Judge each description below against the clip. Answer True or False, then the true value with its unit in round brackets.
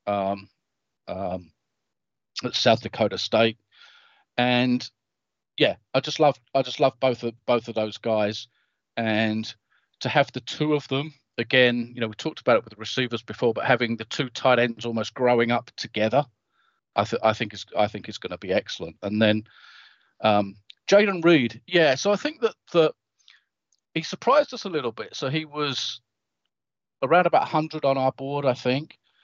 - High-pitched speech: False (125 Hz)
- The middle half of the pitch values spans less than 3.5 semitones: False (4.8 semitones)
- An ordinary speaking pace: True (180 wpm)